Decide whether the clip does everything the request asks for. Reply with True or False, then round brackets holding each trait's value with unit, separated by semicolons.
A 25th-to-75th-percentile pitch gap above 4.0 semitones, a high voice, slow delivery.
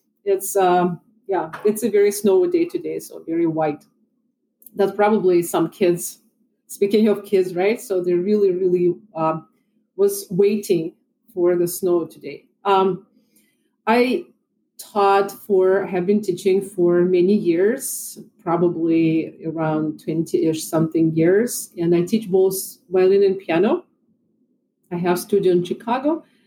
True (4.4 semitones; 195 Hz; 130 wpm)